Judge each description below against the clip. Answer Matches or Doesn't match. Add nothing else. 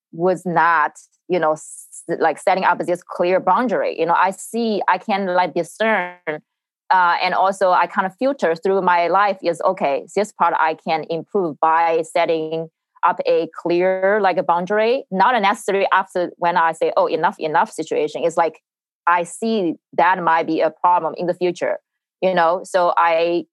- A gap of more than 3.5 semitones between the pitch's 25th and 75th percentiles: Doesn't match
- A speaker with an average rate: Matches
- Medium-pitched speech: Matches